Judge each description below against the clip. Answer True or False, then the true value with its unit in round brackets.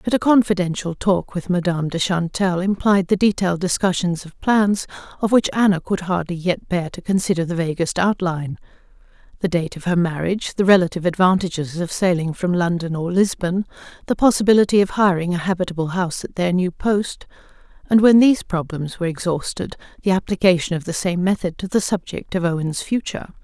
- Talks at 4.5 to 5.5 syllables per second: False (5.9 syllables/s)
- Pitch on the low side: False (180 Hz)